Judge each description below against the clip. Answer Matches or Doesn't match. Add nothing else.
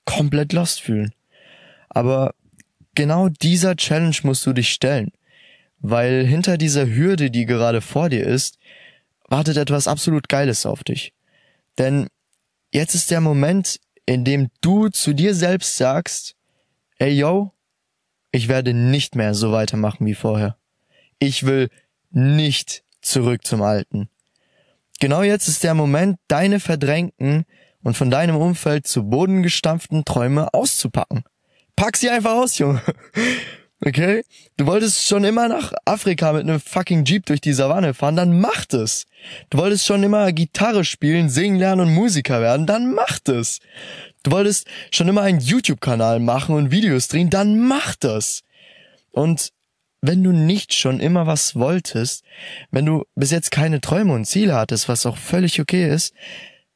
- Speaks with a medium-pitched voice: Matches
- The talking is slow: Doesn't match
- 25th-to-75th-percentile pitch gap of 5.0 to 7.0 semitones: Matches